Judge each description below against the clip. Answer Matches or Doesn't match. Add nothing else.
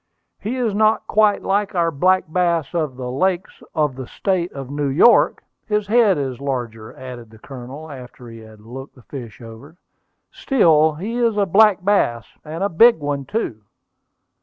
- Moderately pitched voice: Matches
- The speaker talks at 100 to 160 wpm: Doesn't match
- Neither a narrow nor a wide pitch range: Doesn't match